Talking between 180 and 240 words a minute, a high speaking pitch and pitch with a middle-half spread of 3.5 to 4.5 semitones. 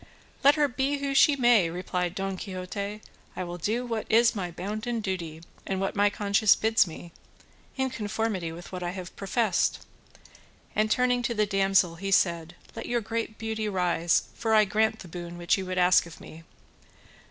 Yes: average, 185 wpm; high, 200 Hz; average, 3.9 semitones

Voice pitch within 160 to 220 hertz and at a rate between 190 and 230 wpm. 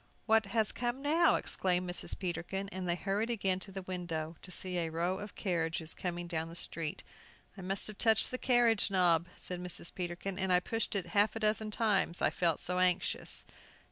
Yes: medium, 185 Hz; average, 200 wpm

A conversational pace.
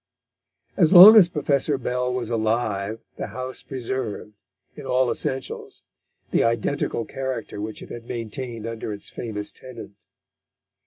No: slow, 130 wpm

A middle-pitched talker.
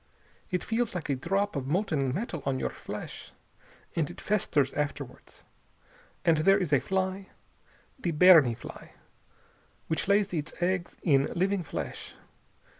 Yes: medium, 175 Hz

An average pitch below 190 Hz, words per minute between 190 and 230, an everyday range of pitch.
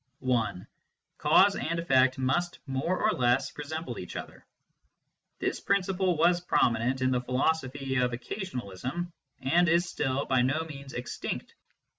No: low, 135 Hz; average, 145 wpm; average, 5.0 semitones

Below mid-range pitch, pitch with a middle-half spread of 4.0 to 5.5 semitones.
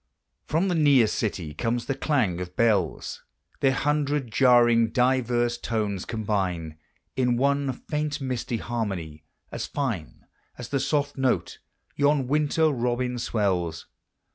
Yes: low, 120 Hz; average, 4.9 semitones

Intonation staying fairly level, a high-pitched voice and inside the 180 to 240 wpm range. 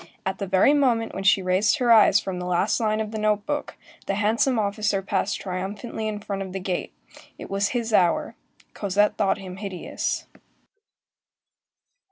No: narrow, 2.3 semitones; high, 205 Hz; average, 170 wpm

